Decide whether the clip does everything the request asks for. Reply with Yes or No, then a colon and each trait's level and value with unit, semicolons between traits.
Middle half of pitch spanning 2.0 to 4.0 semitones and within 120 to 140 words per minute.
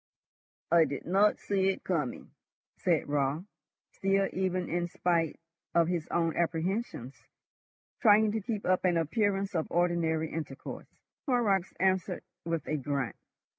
Yes: average, 3.2 semitones; slow, 135 wpm